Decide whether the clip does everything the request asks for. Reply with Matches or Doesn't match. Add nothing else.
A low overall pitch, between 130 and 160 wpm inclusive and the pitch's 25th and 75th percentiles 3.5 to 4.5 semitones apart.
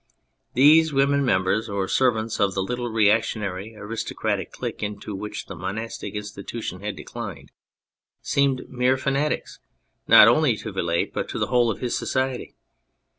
Matches